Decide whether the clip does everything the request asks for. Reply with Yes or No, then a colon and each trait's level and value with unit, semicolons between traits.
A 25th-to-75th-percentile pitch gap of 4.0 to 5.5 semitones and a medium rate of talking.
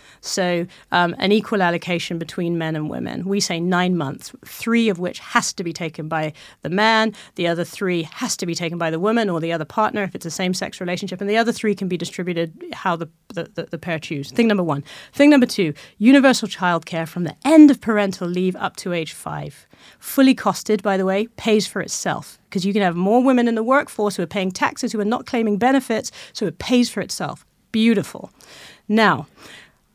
No: average, 4.5 semitones; fast, 215 wpm